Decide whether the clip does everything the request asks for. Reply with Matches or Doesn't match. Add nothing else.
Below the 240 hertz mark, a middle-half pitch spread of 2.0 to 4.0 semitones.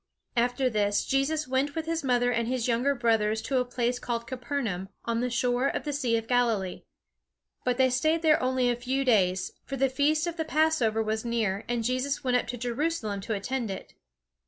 Doesn't match